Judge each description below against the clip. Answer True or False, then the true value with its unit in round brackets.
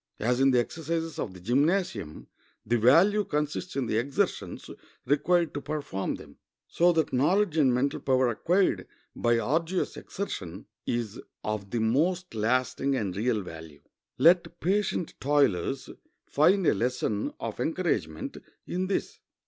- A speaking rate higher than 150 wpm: False (140 wpm)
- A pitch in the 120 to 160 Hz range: True (135 Hz)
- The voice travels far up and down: True (6.7 semitones)